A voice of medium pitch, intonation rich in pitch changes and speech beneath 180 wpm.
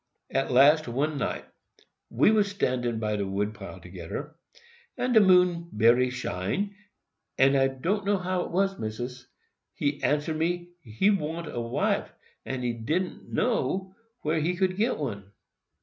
Yes: medium, 145 Hz; wide, 7.4 semitones; average, 150 wpm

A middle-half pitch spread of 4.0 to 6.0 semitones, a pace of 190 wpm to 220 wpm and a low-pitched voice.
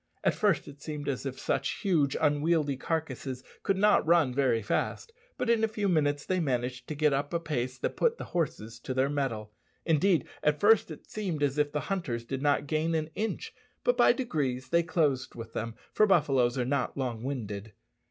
No: average, 4.6 semitones; average, 200 wpm; medium, 145 Hz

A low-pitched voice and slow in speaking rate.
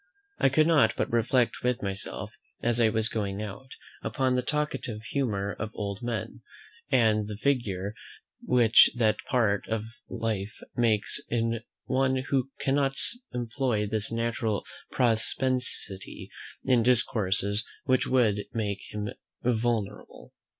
Yes: low, 115 Hz; slow, 130 wpm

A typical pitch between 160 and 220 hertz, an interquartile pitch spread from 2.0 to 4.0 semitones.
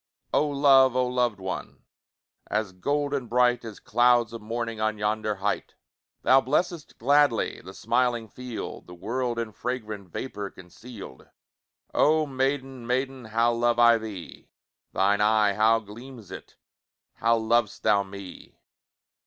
No: low, 115 Hz; average, 3.1 semitones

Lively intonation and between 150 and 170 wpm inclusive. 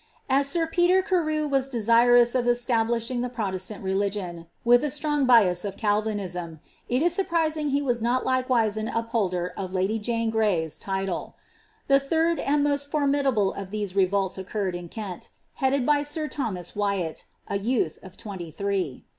Yes: wide, 6.1 semitones; average, 165 wpm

